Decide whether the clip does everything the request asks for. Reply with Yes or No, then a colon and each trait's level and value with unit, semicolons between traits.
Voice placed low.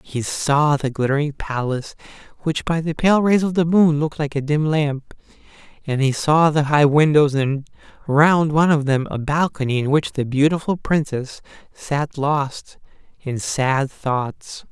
No: medium, 145 Hz